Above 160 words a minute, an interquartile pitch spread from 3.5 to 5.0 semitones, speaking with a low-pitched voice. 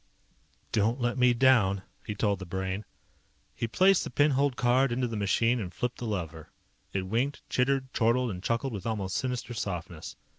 Yes: average, 180 wpm; average, 4.5 semitones; low, 115 Hz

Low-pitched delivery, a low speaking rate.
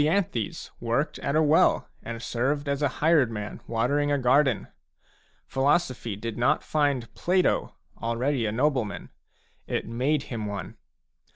Yes: low, 130 Hz; slow, 130 wpm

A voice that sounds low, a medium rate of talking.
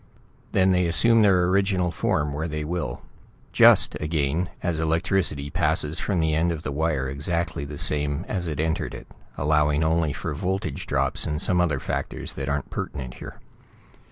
Yes: very low, 80 Hz; average, 170 wpm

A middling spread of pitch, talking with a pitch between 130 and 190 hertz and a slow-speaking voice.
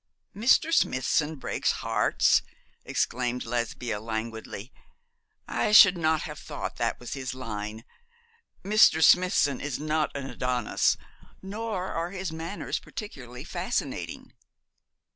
No: wide, 6.8 semitones; medium, 140 Hz; slow, 115 wpm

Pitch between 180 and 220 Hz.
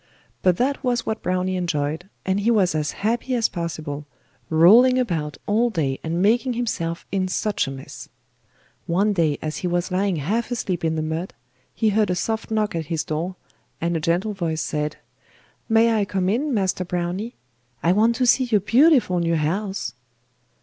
Yes: medium, 185 Hz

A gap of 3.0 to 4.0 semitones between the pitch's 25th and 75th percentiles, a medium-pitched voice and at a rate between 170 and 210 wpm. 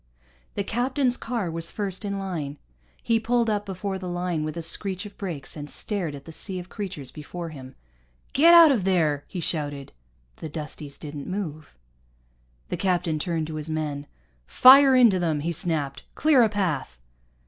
No: average, 5.1 semitones; medium, 175 Hz; average, 175 wpm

